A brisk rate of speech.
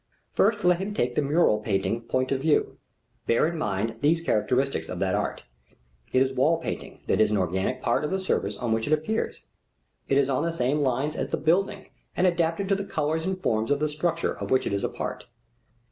Yes: fast, 220 wpm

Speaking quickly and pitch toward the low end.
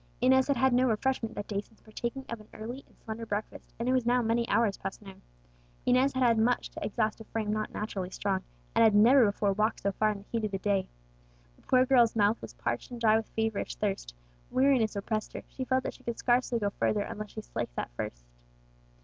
No: fast, 235 wpm; high, 220 Hz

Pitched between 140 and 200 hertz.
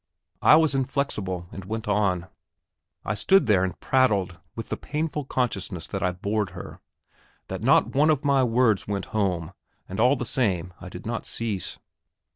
No: low, 105 Hz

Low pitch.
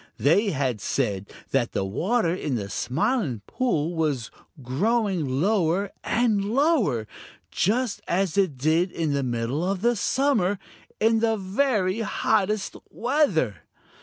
No: medium, 185 Hz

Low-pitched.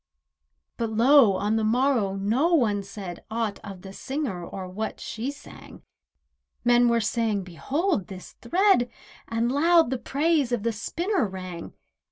No: high, 230 Hz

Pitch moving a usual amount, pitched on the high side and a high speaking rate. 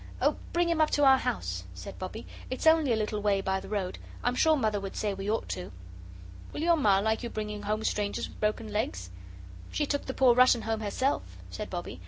Yes: average, 4.7 semitones; high, 215 Hz; fast, 225 wpm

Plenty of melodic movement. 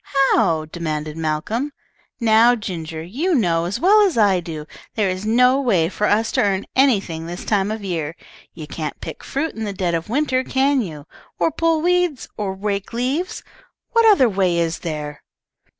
Yes: wide, 7.5 semitones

